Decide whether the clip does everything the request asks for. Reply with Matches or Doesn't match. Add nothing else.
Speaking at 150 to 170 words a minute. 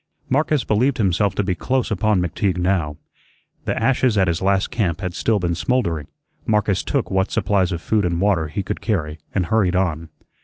Doesn't match